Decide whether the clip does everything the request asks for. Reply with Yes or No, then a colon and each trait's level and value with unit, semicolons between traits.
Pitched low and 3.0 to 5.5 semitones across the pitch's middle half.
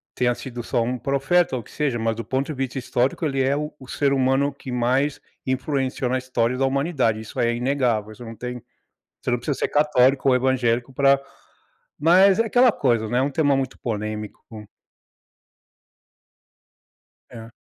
No: low, 130 Hz; narrow, 2.4 semitones